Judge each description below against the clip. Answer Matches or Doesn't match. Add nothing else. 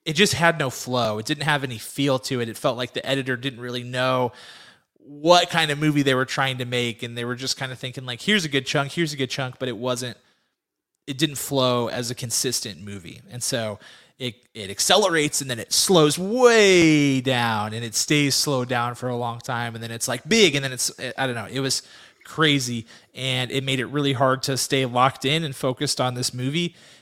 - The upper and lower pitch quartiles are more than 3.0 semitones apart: Doesn't match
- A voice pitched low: Matches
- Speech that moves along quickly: Matches